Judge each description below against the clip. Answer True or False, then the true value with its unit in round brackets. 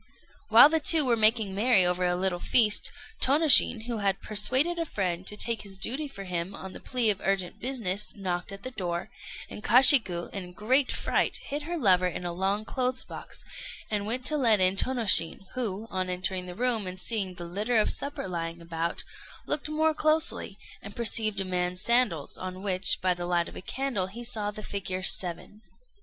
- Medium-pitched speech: False (205 Hz)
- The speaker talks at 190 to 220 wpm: True (200 wpm)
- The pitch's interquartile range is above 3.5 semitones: True (5.1 semitones)